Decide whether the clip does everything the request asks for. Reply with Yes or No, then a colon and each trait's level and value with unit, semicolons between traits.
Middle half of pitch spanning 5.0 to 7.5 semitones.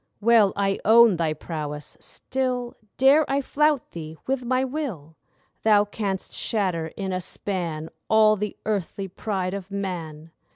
Yes: wide, 5.5 semitones